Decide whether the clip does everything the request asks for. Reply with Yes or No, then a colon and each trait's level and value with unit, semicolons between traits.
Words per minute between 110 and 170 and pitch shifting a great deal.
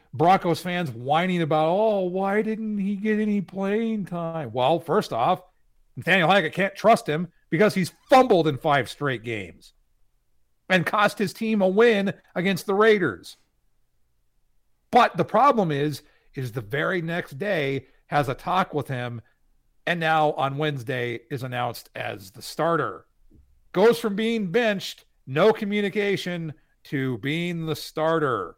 Yes: average, 145 wpm; wide, 6.4 semitones